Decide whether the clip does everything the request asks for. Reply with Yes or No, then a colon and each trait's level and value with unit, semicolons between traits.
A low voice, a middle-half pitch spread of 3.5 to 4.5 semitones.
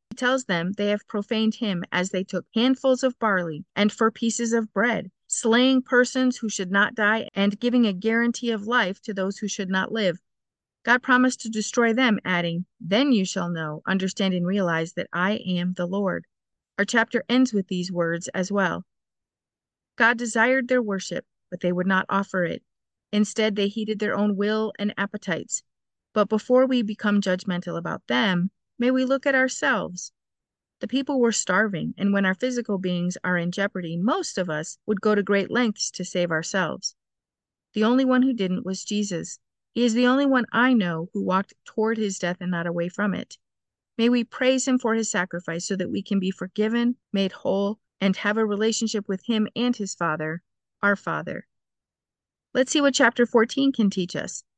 No: high, 205 Hz; average, 4.1 semitones